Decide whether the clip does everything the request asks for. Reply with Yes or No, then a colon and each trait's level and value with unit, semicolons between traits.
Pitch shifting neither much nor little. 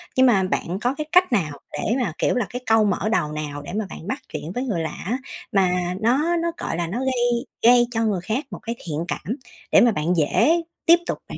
No: wide, 6.1 semitones